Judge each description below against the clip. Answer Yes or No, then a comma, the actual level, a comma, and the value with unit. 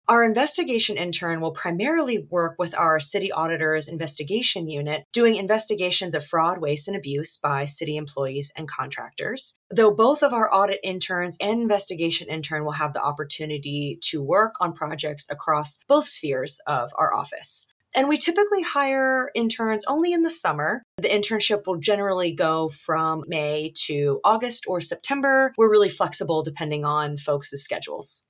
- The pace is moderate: Yes, average, 155 wpm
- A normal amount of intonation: No, wide, 6.2 semitones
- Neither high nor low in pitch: Yes, medium, 175 Hz